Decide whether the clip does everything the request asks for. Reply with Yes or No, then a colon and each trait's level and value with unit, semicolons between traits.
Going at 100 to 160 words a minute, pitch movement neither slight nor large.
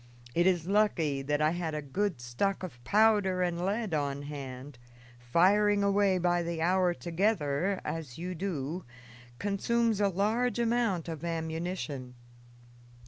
Yes: average, 140 wpm; average, 4.9 semitones